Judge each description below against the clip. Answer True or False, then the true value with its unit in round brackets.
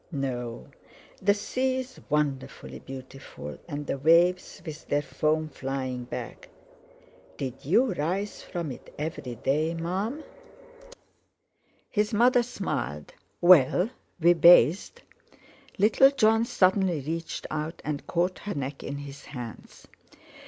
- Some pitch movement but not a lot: False (6.1 semitones)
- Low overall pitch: False (160 Hz)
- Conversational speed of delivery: False (115 wpm)